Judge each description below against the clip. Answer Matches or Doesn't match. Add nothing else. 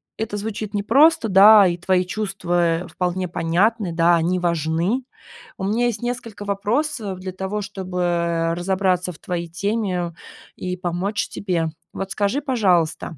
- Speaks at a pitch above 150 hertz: Matches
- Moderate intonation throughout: Matches